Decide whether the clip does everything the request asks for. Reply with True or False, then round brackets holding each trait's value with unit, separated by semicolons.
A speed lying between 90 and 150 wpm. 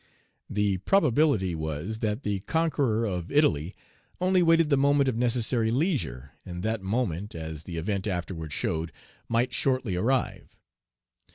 True (135 wpm)